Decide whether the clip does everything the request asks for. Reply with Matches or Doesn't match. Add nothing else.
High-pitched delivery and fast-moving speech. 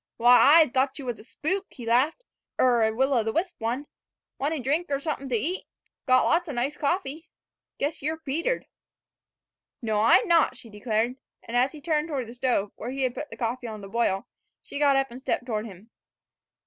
Matches